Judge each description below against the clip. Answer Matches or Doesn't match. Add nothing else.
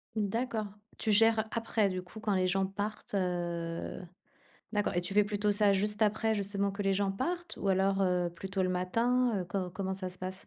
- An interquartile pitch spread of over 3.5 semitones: Doesn't match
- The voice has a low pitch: Doesn't match